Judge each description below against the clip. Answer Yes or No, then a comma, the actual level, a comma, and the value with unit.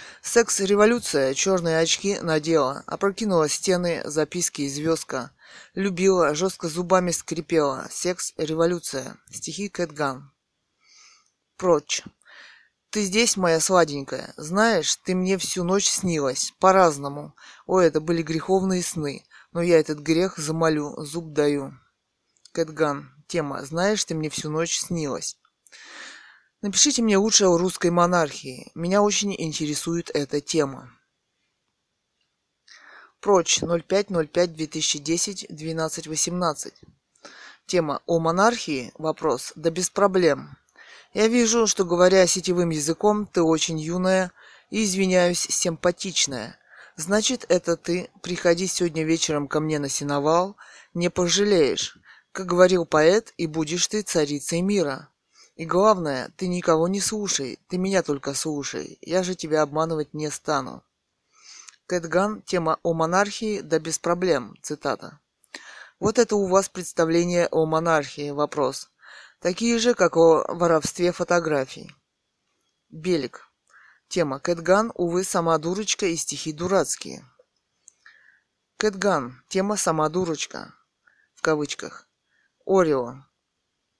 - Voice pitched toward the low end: No, medium, 170 Hz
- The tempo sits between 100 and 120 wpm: Yes, slow, 110 wpm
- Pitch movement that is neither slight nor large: Yes, average, 3.2 semitones